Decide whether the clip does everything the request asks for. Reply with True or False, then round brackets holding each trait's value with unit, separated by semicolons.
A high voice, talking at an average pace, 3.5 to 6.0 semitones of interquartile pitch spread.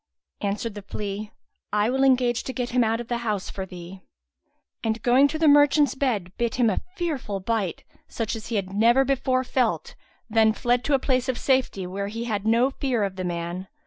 False (230 Hz; 210 wpm; 4.2 semitones)